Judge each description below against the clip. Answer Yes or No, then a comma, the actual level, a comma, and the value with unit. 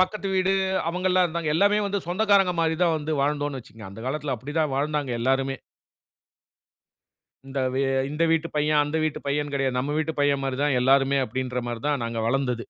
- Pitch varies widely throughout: No, average, 3.5 semitones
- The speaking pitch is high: No, medium, 145 Hz